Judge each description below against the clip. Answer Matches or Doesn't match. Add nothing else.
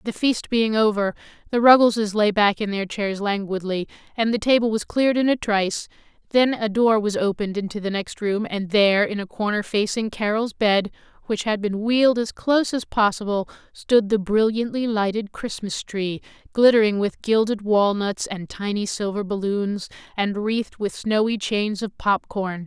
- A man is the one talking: Doesn't match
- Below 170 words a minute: Doesn't match